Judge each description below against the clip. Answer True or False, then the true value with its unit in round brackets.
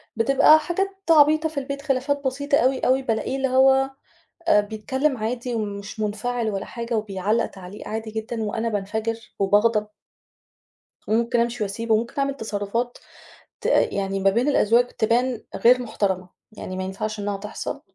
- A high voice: True (230 Hz)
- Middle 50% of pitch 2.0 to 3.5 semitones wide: False (3.9 semitones)